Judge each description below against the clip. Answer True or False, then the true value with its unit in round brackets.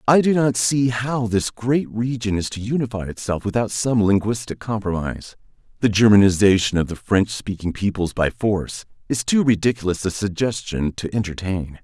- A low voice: True (110 Hz)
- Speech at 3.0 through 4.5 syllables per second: False (5.1 syllables/s)